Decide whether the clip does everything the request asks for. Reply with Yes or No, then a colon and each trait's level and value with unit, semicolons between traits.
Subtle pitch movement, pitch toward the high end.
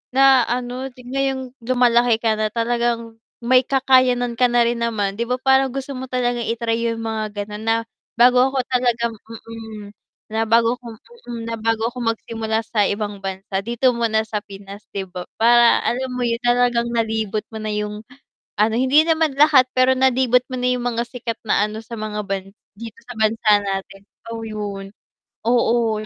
Yes: narrow, 2.3 semitones; high, 230 Hz